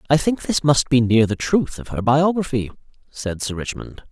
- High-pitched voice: No, low, 135 Hz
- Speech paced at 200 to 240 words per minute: Yes, fast, 205 wpm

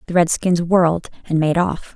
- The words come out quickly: No, average, 185 wpm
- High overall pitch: No, medium, 170 Hz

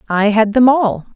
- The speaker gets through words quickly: Yes, fast, 210 wpm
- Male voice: No, female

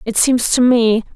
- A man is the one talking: No, female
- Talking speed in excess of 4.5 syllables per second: No, 4.3 syllables/s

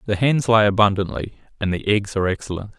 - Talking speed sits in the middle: Yes, average, 195 wpm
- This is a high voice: No, low, 105 Hz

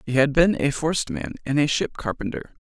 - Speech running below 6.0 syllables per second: Yes, 5.7 syllables/s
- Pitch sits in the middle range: Yes, medium, 145 Hz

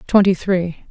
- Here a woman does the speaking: Yes, female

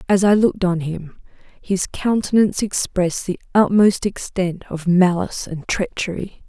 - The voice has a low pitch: No, medium, 185 Hz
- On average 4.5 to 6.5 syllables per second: Yes, 4.9 syllables/s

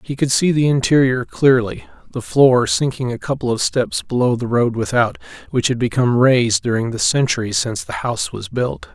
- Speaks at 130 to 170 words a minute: No, average, 190 wpm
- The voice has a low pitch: Yes, low, 125 Hz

